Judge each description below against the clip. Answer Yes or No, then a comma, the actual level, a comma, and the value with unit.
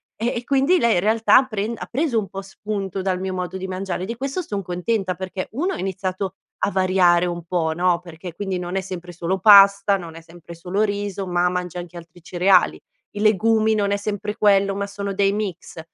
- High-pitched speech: Yes, high, 195 Hz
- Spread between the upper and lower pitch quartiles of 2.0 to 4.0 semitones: Yes, narrow, 2.6 semitones